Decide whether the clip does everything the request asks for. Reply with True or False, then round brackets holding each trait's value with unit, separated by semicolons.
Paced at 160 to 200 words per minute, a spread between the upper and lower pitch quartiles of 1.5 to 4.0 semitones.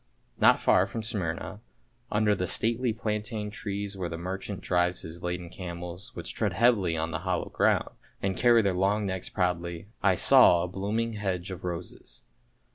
True (165 wpm; 3.0 semitones)